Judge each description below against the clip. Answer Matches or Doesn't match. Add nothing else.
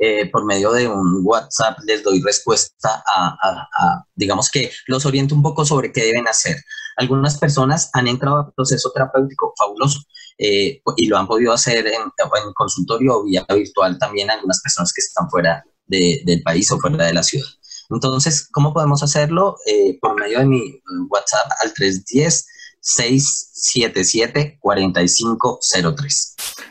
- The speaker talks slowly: Doesn't match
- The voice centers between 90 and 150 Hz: Matches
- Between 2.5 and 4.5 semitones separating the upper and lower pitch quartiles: Doesn't match